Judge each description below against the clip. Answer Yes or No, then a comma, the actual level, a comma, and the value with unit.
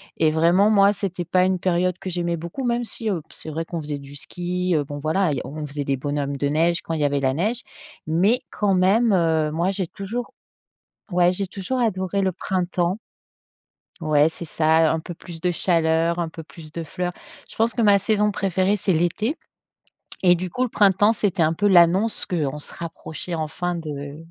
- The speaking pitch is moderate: Yes, medium, 175 Hz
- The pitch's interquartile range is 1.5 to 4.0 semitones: Yes, average, 3.5 semitones